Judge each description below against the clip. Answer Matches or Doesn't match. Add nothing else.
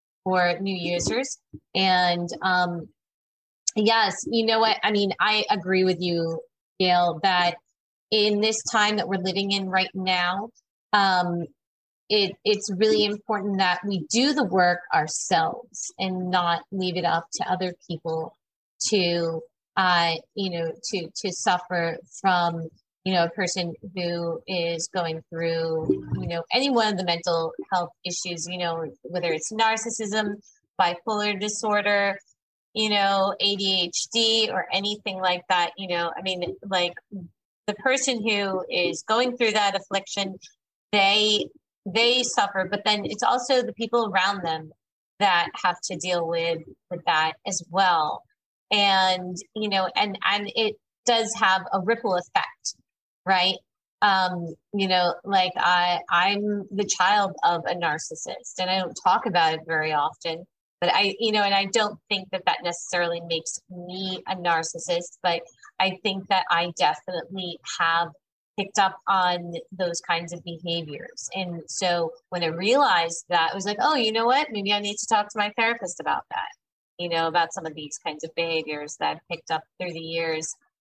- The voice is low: Doesn't match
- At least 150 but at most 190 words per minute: Matches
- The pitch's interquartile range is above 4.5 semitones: Doesn't match